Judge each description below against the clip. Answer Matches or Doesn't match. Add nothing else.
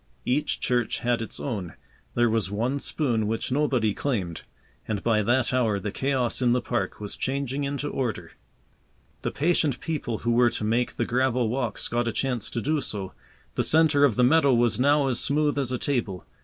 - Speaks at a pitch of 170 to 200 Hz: Doesn't match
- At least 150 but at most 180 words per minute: Doesn't match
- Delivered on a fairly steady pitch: Doesn't match